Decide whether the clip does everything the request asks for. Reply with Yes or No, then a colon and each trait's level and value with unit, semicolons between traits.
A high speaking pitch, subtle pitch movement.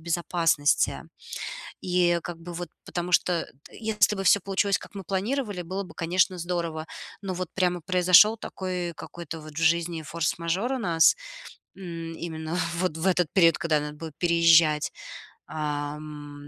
No: medium, 170 Hz; narrow, 2.3 semitones